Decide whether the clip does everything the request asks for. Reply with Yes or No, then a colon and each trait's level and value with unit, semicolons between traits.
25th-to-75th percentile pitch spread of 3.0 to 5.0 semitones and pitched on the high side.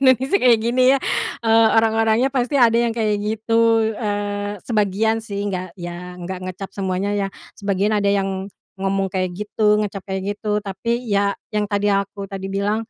No: narrow, 2.4 semitones; high, 205 Hz